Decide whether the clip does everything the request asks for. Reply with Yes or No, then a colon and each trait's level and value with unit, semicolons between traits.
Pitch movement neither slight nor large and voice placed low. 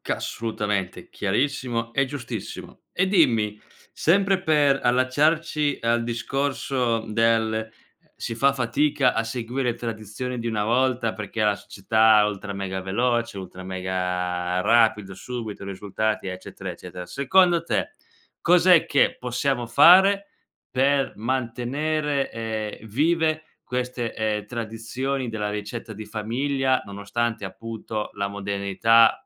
Yes: average, 4.2 semitones; low, 115 Hz